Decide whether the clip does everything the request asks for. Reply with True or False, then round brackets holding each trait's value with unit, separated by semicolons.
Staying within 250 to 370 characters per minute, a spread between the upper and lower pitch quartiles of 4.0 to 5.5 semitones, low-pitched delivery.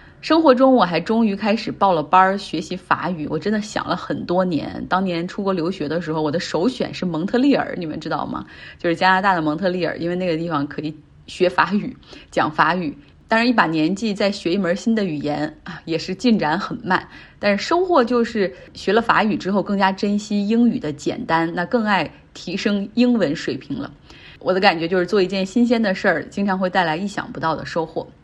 False (320 characters per minute; 4.3 semitones; 185 Hz)